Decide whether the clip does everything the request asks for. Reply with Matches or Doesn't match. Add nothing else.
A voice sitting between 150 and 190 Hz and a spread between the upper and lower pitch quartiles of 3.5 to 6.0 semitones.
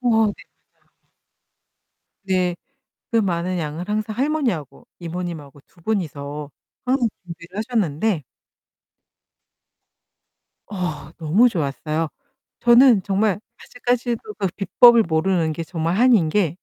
Matches